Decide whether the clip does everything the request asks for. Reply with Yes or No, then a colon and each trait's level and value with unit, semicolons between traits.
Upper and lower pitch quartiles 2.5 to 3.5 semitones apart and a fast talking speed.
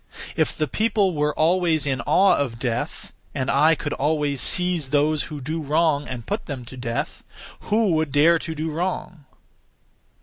No: average, 3.1 semitones; average, 170 wpm